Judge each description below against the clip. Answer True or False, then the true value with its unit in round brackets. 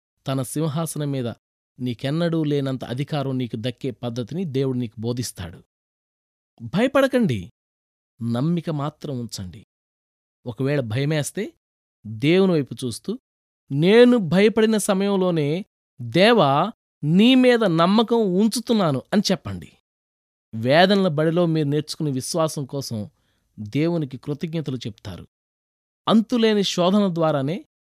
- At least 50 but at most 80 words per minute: False (90 wpm)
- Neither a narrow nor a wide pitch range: False (7.3 semitones)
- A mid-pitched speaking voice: True (145 Hz)